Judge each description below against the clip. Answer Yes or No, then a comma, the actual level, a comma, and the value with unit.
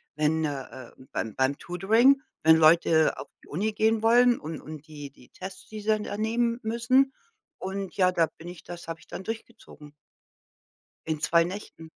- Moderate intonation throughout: No, wide, 5.8 semitones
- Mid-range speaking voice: Yes, medium, 180 Hz